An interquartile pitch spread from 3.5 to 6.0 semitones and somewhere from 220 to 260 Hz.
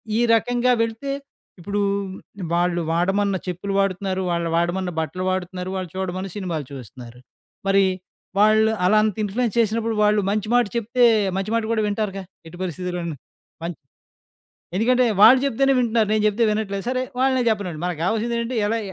No: average, 3.9 semitones; high, 200 Hz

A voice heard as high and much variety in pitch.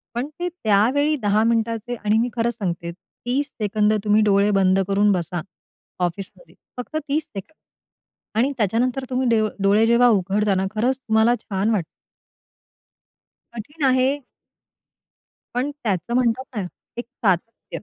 No: high, 220 Hz; average, 3.8 semitones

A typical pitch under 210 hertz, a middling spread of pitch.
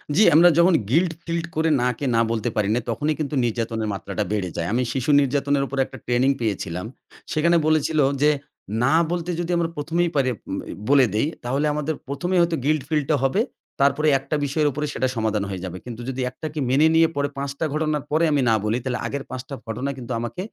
Yes: medium, 140 Hz; average, 4.5 semitones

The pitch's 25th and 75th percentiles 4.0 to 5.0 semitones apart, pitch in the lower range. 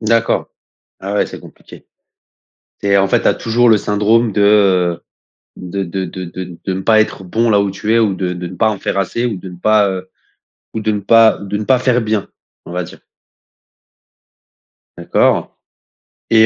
No: average, 2.7 semitones; low, 105 Hz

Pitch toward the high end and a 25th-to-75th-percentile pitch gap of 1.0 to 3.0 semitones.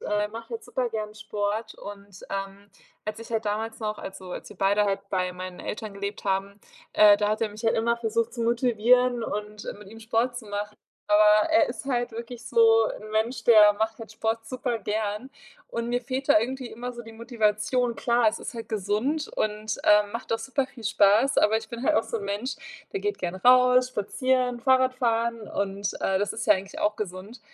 Yes: high, 220 Hz; narrow, 2.5 semitones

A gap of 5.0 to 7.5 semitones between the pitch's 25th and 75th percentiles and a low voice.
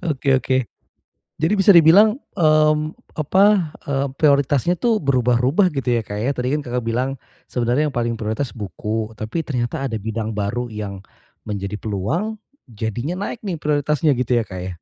Yes: wide, 5.5 semitones; low, 130 Hz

